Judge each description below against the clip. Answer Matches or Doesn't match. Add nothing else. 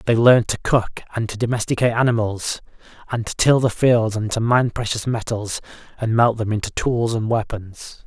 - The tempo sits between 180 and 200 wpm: Matches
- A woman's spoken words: Doesn't match